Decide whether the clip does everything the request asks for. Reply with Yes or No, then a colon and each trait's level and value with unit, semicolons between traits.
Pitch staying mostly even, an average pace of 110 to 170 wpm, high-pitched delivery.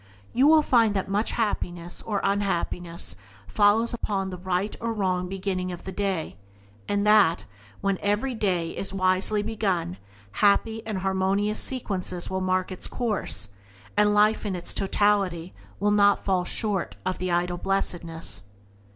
Yes: narrow, 2.3 semitones; average, 150 wpm; high, 195 Hz